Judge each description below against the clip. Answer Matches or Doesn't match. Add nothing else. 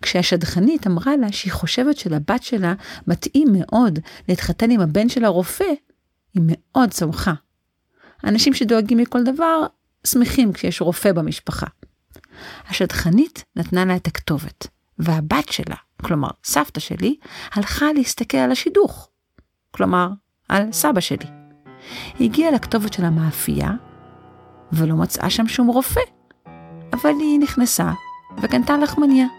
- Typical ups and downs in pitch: Doesn't match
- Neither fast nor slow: Matches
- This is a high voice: Matches